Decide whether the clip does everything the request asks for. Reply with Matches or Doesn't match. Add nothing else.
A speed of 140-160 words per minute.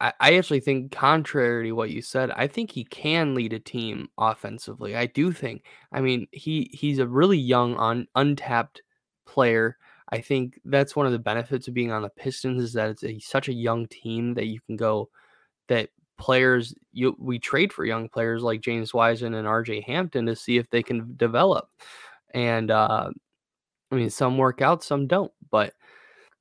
Doesn't match